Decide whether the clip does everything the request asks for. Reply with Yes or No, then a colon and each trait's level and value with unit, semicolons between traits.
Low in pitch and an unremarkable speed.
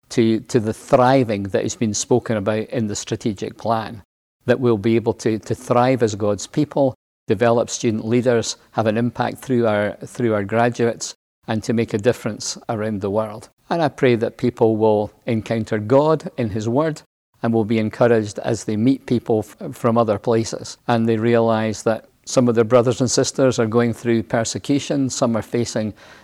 Yes: low, 115 Hz; average, 185 wpm